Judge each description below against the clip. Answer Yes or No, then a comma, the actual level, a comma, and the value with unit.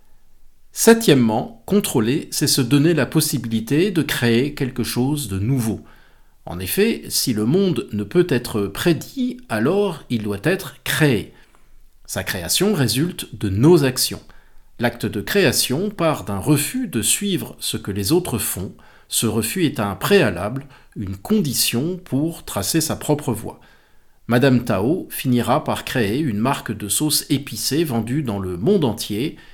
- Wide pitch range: Yes, wide, 6.1 semitones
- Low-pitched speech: Yes, low, 130 Hz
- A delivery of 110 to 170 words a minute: Yes, average, 150 wpm